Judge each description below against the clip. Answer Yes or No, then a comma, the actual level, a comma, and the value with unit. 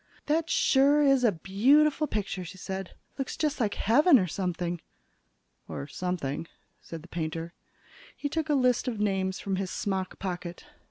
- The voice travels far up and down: Yes, wide, 7.3 semitones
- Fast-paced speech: No, average, 160 wpm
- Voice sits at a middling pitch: No, high, 195 Hz